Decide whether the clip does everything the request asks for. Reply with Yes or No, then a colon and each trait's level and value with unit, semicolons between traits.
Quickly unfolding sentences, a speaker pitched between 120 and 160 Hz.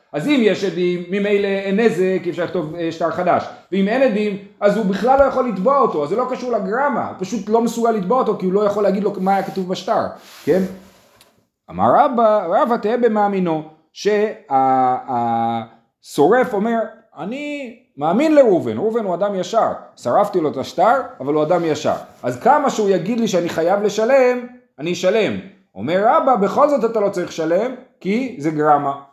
No: fast, 180 wpm; high, 205 Hz